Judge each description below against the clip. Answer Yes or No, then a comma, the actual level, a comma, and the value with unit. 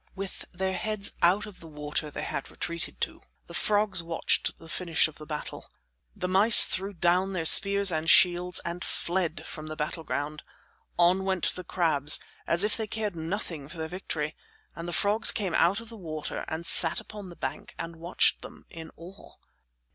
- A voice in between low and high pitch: Yes, medium, 175 Hz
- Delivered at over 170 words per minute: Yes, average, 185 wpm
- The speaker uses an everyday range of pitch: Yes, average, 3.2 semitones